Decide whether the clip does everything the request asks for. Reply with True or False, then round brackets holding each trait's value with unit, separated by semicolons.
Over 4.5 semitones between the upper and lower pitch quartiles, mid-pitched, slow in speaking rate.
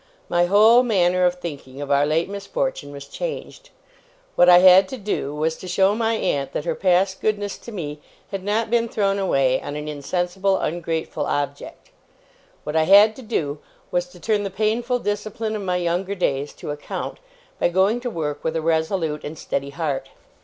False (5.2 semitones; 180 Hz; 190 wpm)